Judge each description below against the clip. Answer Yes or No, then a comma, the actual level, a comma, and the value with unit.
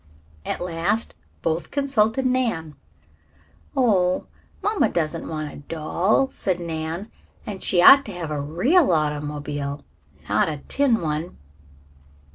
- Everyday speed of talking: No, slow, 120 wpm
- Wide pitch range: Yes, wide, 6.4 semitones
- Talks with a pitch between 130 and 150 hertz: No, medium, 170 Hz